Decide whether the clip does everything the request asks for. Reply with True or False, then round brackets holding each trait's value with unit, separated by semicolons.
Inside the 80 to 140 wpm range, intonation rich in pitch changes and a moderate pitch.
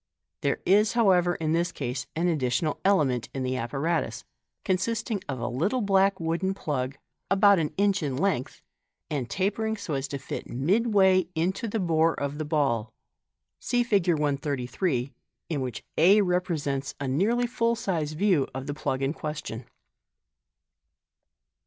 False (150 wpm; 6.2 semitones; 165 Hz)